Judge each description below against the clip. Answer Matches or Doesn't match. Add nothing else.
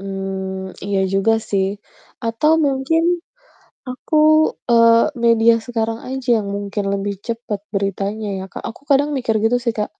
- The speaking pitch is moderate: Doesn't match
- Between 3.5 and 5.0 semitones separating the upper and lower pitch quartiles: Matches